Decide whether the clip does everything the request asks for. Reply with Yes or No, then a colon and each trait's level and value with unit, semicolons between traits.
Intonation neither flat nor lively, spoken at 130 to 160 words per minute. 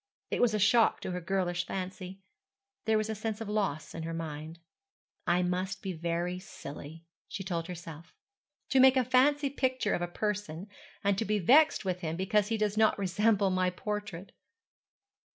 No: average, 3.6 semitones; average, 180 wpm